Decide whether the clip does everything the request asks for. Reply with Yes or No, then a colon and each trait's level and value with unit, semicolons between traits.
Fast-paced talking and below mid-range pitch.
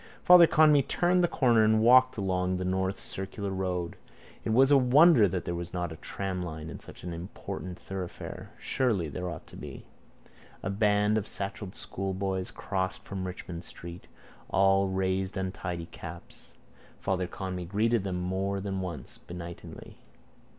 No: average, 155 wpm; very low, 95 Hz